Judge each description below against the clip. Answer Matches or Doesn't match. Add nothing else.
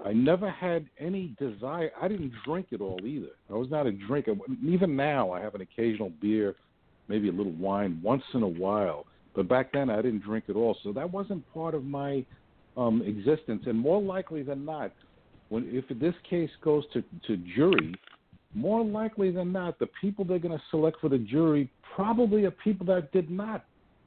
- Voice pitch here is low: Doesn't match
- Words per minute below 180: Doesn't match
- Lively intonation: Matches